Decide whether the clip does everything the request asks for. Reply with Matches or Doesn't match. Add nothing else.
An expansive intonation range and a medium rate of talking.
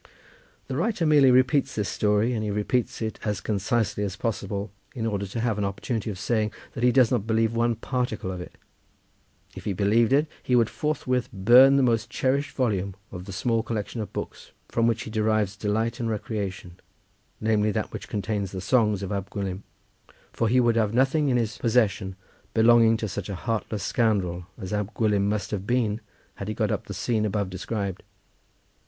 Doesn't match